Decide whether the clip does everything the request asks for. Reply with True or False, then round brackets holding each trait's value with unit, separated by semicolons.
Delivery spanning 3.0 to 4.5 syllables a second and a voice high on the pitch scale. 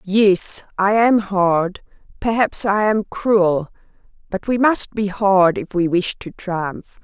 True (3.3 syllables/s; 195 Hz)